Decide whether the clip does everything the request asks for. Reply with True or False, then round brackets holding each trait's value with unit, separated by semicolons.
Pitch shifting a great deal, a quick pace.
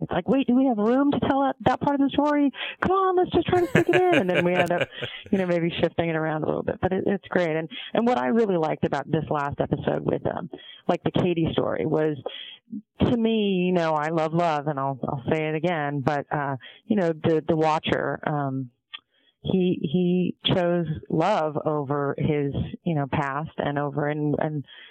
True (5.8 semitones; 220 wpm)